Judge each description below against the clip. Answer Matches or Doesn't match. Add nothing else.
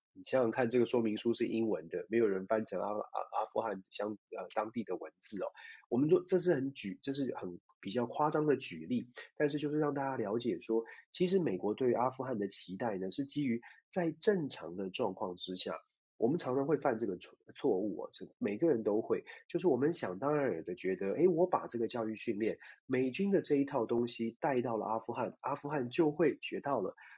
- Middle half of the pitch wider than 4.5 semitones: Matches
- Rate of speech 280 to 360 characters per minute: Matches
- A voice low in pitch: Matches